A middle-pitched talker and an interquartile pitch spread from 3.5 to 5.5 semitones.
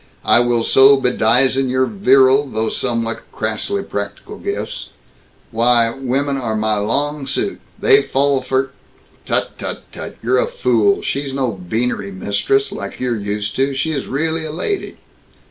No: low, 130 Hz; average, 3.9 semitones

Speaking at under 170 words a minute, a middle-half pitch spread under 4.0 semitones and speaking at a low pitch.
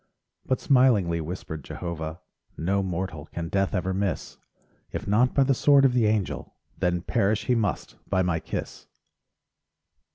No: average, 150 wpm; average, 5.1 semitones; very low, 95 Hz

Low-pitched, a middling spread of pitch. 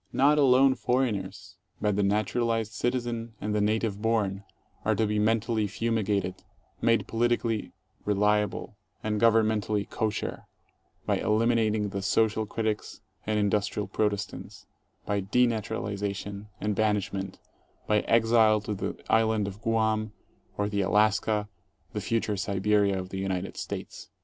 No: low, 105 Hz; narrow, 1.7 semitones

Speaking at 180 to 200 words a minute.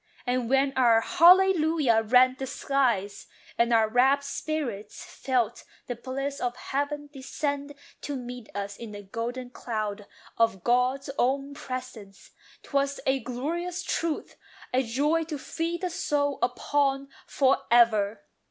No: slow, 135 wpm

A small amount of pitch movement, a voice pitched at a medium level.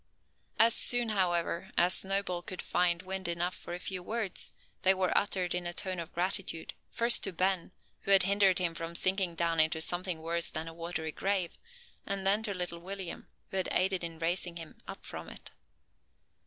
Yes: narrow, 2.2 semitones; medium, 180 Hz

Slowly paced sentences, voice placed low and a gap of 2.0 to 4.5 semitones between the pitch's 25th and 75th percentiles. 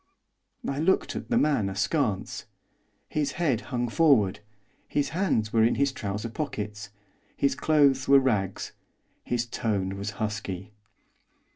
No: slow, 130 wpm; low, 120 Hz; wide, 5.5 semitones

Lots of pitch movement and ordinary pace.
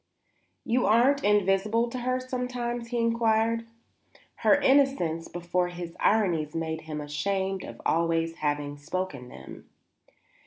No: wide, 6.2 semitones; slow, 120 wpm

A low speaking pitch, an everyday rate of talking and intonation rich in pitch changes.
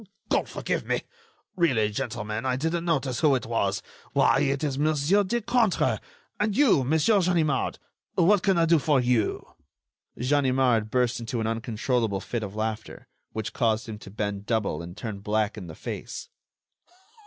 Yes: low, 125 Hz; average, 160 wpm; wide, 6.3 semitones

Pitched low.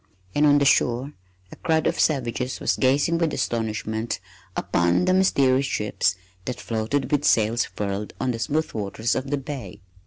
Yes: low, 130 Hz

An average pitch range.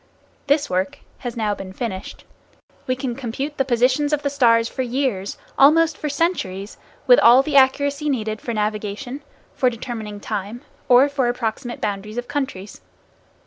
Yes: average, 4.6 semitones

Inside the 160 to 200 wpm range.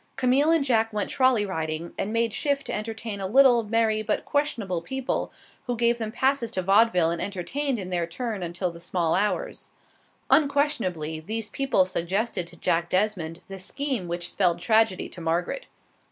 Yes: average, 170 wpm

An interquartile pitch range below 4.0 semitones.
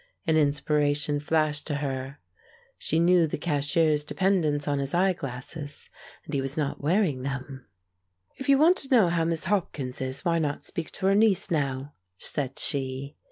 Yes: average, 3.5 semitones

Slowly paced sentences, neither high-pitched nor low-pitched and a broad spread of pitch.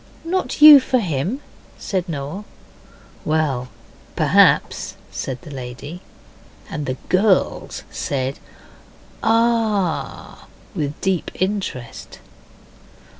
Yes: slow, 85 wpm; medium, 175 Hz; wide, 7.3 semitones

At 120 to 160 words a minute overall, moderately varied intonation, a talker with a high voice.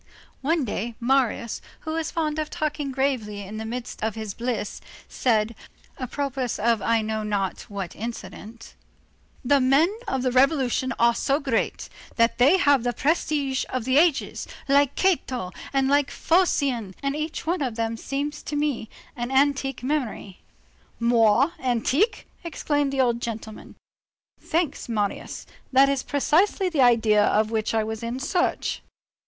Yes: average, 150 wpm; average, 4.1 semitones; very high, 260 Hz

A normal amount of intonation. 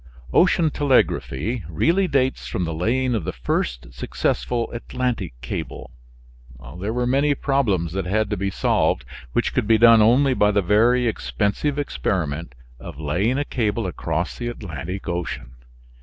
No: wide, 6.4 semitones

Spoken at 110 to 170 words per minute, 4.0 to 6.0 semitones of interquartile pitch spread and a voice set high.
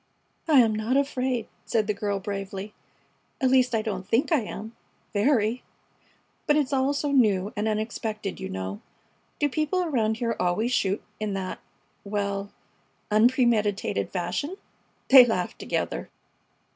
Yes: average, 140 wpm; average, 4.3 semitones; high, 220 Hz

